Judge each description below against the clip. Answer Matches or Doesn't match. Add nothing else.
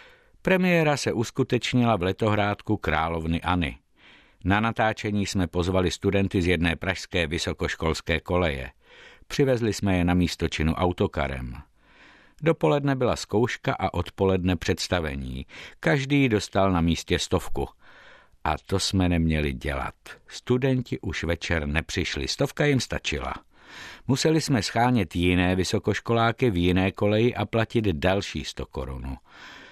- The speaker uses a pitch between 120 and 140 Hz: Doesn't match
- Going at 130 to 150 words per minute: Doesn't match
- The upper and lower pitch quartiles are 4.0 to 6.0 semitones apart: Matches